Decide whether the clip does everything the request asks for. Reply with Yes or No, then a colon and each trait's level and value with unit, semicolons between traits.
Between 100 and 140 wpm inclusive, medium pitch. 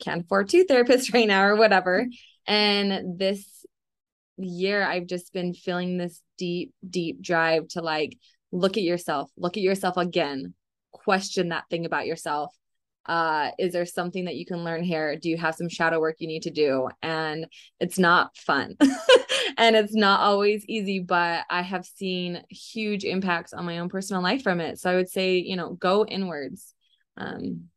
No: average, 180 wpm; medium, 180 Hz